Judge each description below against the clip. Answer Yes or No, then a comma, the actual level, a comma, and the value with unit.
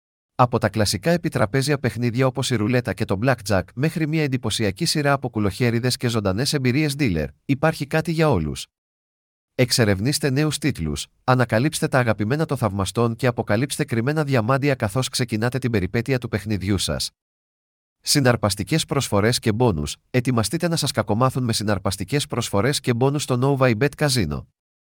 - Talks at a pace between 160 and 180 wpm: No, average, 150 wpm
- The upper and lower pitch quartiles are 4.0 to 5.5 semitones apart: Yes, average, 5.1 semitones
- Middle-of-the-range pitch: No, low, 125 Hz